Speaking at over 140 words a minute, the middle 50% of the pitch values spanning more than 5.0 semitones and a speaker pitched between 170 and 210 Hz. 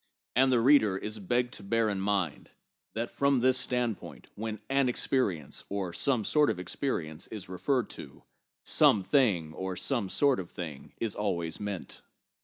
No: average, 165 wpm; wide, 5.4 semitones; low, 105 Hz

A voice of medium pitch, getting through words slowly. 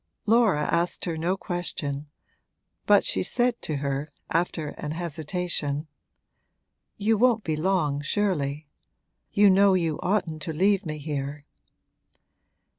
Yes: medium, 165 Hz; slow, 120 wpm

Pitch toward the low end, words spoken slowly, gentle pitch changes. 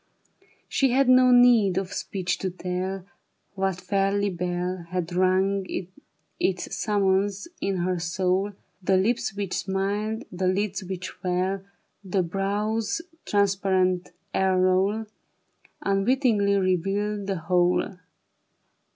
No: high, 195 Hz; slow, 110 wpm; narrow, 1.7 semitones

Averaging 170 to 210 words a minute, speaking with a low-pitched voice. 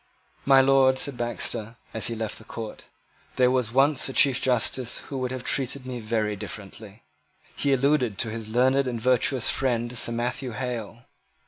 Yes: average, 175 wpm; low, 125 Hz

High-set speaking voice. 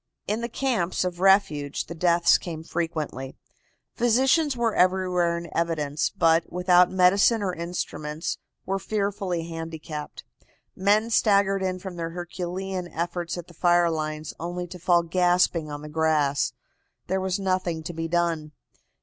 No: medium, 175 Hz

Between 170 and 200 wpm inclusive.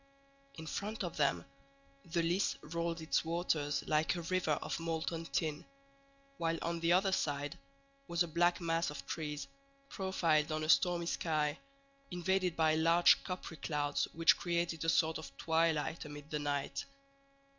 No: average, 155 wpm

